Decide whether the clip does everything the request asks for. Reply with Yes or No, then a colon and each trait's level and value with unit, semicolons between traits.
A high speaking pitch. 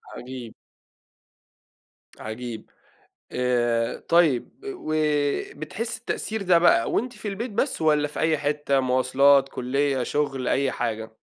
No: medium, 140 Hz